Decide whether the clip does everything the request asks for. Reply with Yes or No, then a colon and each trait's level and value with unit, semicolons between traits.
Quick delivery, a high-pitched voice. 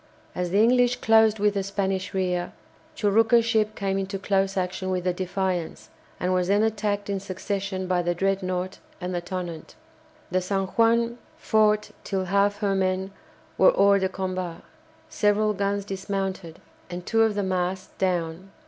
No: average, 160 wpm; high, 195 Hz